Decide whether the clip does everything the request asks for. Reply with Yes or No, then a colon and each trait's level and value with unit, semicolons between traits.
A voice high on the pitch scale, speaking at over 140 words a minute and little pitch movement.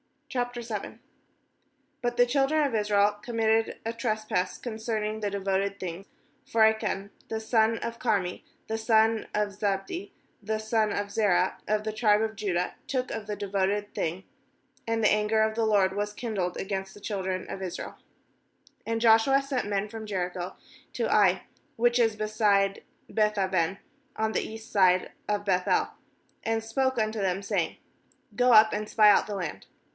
Yes: high, 215 Hz; average, 165 wpm; narrow, 2.2 semitones